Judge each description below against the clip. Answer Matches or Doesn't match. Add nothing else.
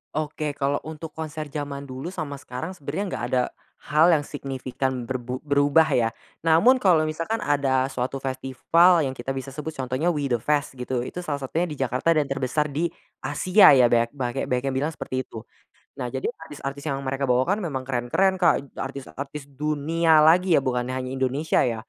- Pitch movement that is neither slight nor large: Matches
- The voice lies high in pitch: Doesn't match